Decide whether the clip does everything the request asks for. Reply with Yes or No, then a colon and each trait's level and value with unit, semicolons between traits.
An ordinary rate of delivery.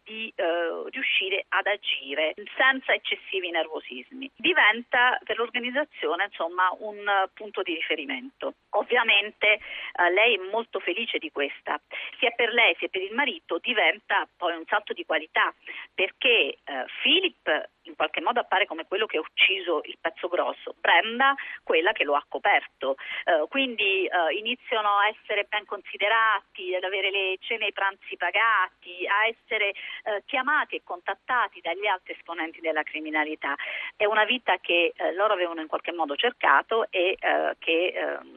Yes: average, 160 wpm